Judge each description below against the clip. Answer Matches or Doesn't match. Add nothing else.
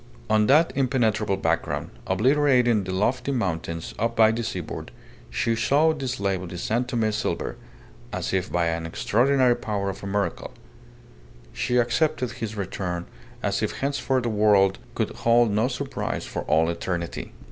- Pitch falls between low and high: Doesn't match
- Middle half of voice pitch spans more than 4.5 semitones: Matches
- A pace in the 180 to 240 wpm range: Doesn't match